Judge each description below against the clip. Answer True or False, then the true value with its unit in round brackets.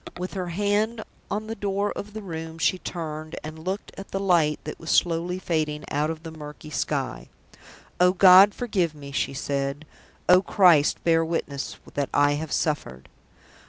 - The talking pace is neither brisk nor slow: True (170 wpm)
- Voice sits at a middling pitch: True (165 Hz)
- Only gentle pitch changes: False (4.0 semitones)